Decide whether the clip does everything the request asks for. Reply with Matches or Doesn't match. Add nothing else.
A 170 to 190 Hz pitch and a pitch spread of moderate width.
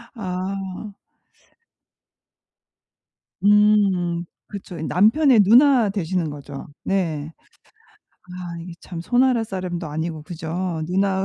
Matches